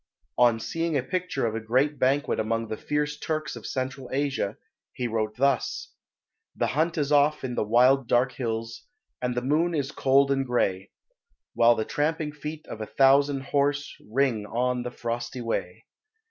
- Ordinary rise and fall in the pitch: Yes, average, 3.6 semitones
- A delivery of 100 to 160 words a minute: No, average, 175 wpm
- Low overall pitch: Yes, low, 130 Hz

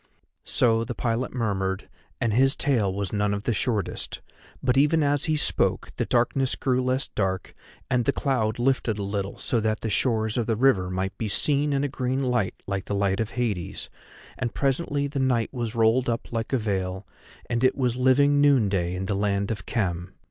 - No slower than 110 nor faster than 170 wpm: No, average, 200 wpm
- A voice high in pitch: No, low, 115 Hz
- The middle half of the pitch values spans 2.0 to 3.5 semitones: No, average, 4.5 semitones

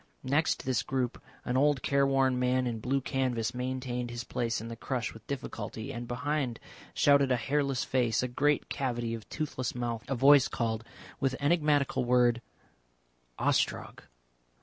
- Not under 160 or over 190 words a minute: No, average, 150 wpm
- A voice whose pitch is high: No, low, 125 Hz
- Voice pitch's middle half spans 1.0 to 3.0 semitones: Yes, narrow, 2.5 semitones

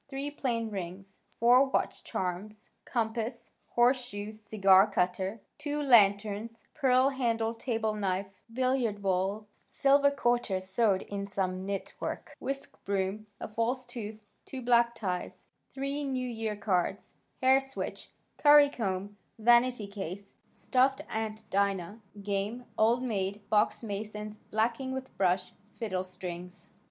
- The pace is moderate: No, slow, 125 wpm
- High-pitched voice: Yes, high, 220 Hz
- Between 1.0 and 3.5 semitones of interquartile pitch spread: No, average, 4.0 semitones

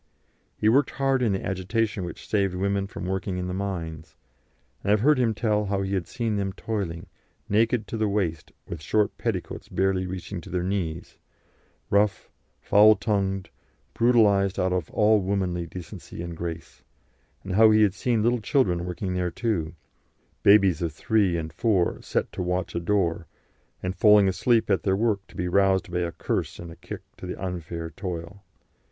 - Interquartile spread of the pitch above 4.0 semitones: No, average, 3.0 semitones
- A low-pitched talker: Yes, very low, 95 Hz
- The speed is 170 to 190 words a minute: Yes, average, 180 wpm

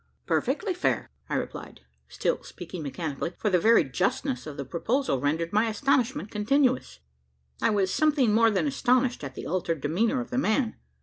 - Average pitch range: No, wide, 7.5 semitones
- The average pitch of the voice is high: Yes, high, 215 Hz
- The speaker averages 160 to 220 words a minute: Yes, average, 170 wpm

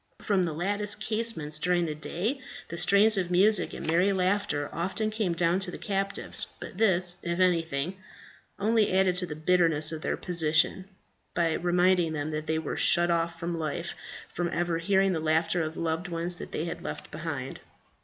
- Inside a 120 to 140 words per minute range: No, average, 185 wpm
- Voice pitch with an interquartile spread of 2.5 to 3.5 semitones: Yes, average, 2.9 semitones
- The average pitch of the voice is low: No, medium, 175 Hz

